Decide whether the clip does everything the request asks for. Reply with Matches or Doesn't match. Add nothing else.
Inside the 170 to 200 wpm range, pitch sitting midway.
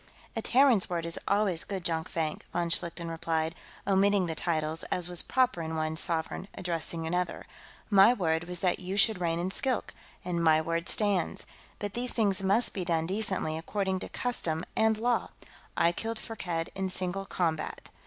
Matches